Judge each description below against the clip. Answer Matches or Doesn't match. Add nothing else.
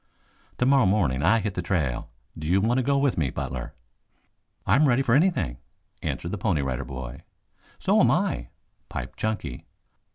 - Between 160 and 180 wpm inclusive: Matches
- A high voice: Doesn't match